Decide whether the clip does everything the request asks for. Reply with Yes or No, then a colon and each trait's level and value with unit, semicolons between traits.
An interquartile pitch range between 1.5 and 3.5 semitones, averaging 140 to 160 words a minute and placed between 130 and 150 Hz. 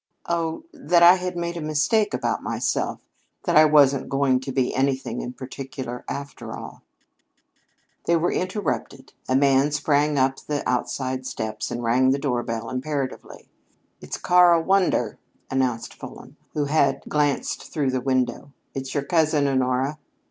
Yes: average, 3.1 semitones; average, 150 wpm; medium, 140 Hz